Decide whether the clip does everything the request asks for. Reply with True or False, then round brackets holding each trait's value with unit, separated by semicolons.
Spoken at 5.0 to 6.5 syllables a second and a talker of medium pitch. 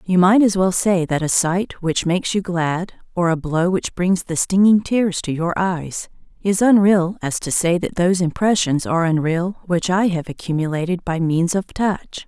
False (4.6 syllables/s; 180 Hz)